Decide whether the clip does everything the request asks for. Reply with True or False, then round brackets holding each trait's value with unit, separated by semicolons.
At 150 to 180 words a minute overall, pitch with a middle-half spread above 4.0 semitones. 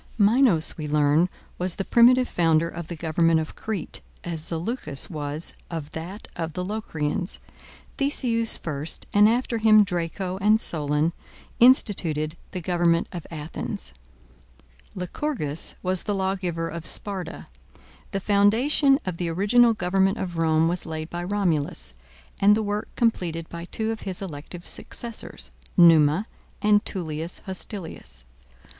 False (135 wpm; 4.4 semitones)